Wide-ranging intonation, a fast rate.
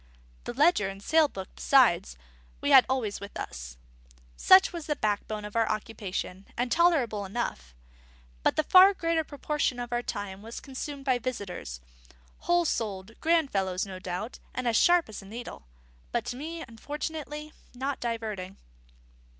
No: wide, 6.8 semitones; average, 160 wpm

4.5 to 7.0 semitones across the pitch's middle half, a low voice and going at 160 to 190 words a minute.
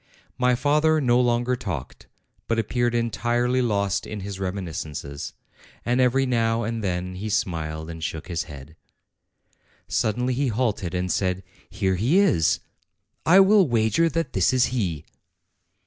No: wide, 5.4 semitones; low, 115 Hz; average, 145 wpm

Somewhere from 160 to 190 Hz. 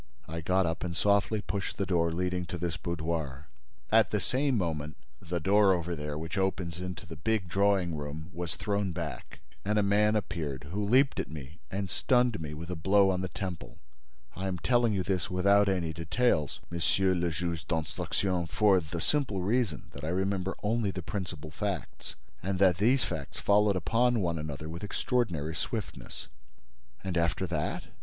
No: very low, 90 Hz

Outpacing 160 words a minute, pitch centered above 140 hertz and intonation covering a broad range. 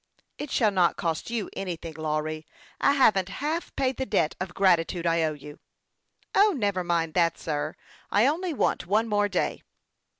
Yes: average, 180 wpm; medium, 185 Hz; wide, 5.8 semitones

